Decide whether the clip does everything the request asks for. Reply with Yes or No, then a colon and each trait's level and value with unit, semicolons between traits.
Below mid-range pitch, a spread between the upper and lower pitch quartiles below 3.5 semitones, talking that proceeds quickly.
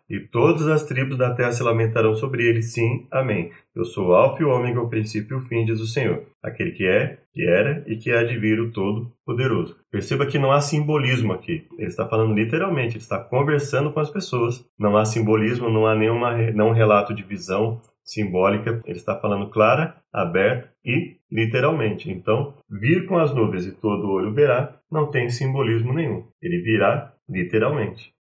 No: low, 115 Hz; average, 4.3 semitones; fast, 190 wpm